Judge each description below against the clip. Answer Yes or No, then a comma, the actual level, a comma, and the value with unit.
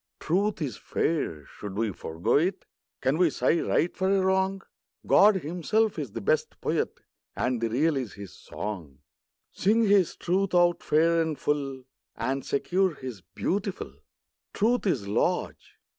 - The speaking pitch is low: No, medium, 160 Hz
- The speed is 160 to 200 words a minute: No, average, 150 wpm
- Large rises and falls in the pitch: Yes, wide, 7.4 semitones